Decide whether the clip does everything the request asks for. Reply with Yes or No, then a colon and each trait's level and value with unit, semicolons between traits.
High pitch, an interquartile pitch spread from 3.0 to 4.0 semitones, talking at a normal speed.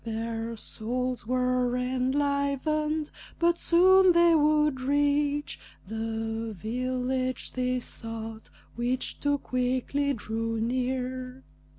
No: very high, 255 Hz; average, 3.7 semitones; slow, 90 wpm